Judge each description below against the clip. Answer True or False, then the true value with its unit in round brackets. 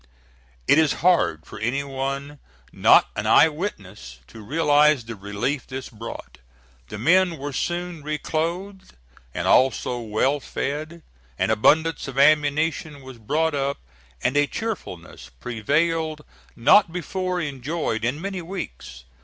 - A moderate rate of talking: False (130 wpm)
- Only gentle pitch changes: False (5.0 semitones)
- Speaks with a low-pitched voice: False (145 Hz)